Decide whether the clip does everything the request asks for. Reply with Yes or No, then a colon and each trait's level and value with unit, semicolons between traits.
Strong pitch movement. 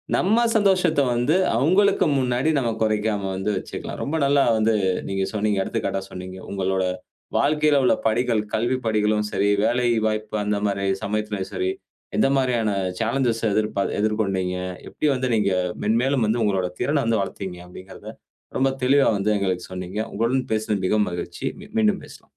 No: average, 4.7 semitones